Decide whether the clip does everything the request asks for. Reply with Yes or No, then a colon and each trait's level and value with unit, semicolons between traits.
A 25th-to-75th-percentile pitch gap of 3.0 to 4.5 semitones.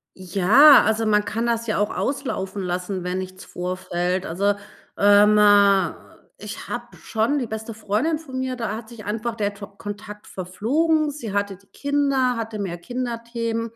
Yes: average, 3.3 semitones